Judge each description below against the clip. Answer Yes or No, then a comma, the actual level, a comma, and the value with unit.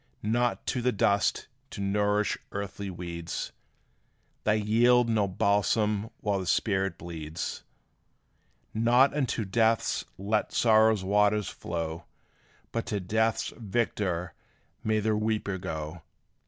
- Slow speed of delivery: Yes, slow, 115 wpm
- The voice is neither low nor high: No, low, 105 Hz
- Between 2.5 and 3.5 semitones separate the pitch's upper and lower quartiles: Yes, average, 2.9 semitones